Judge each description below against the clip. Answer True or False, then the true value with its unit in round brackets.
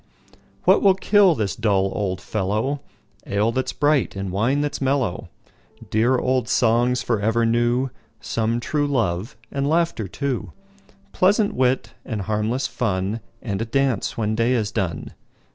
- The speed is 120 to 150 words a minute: True (135 wpm)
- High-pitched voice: False (120 Hz)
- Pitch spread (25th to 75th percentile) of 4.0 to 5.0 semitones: True (4.5 semitones)